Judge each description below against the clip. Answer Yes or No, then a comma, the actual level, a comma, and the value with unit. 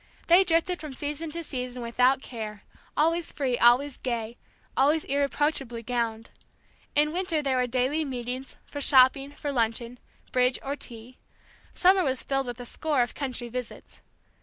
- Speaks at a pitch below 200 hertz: No, very high, 265 Hz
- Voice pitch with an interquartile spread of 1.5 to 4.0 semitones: Yes, average, 3.4 semitones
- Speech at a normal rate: Yes, average, 155 wpm